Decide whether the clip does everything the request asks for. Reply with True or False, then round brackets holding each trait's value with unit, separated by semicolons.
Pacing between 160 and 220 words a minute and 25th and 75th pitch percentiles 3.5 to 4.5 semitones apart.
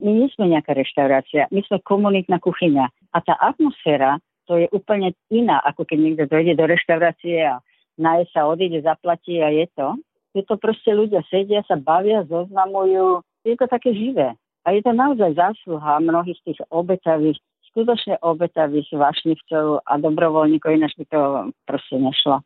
True (165 wpm; 4.1 semitones)